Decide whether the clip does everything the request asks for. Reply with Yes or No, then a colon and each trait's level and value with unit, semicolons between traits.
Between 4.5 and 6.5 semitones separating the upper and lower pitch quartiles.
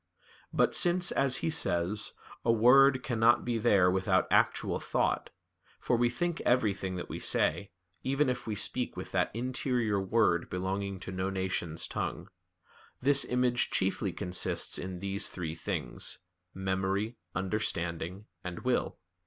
Yes: average, 4.9 semitones